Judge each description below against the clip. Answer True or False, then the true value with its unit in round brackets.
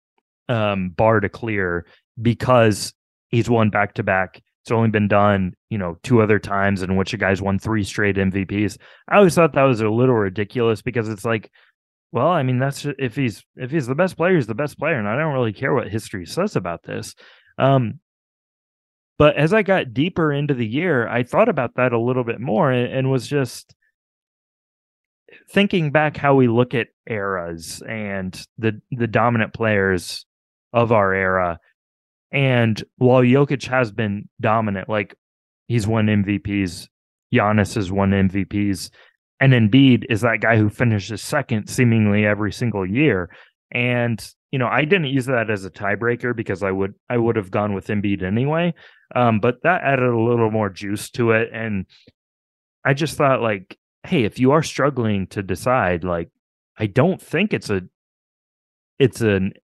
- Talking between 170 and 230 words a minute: True (175 wpm)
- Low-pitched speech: True (115 Hz)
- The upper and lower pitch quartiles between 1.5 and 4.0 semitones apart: False (4.4 semitones)